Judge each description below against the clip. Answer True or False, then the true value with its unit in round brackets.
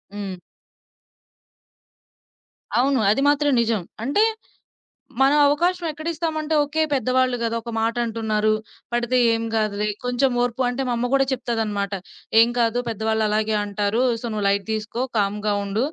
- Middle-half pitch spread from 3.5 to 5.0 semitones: True (4.1 semitones)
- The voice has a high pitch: True (230 Hz)